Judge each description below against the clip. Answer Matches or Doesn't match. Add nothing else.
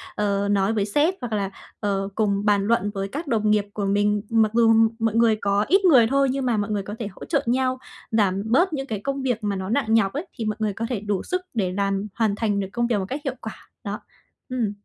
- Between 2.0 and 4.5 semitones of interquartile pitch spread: Matches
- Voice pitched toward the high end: Matches